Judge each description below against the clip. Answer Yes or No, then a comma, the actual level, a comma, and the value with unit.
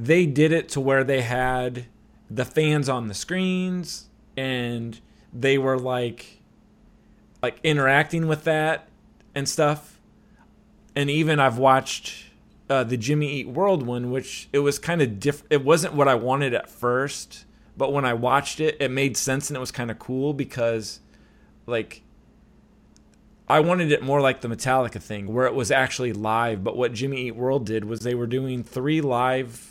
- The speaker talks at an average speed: Yes, average, 175 wpm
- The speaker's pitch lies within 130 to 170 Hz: Yes, low, 135 Hz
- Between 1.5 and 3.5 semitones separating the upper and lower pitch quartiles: Yes, average, 2.9 semitones